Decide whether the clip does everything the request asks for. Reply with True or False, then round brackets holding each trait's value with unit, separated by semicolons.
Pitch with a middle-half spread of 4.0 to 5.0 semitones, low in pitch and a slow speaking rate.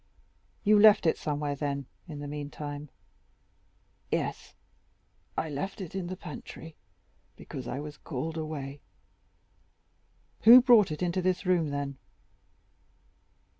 False (4.3 semitones; 155 Hz; 120 wpm)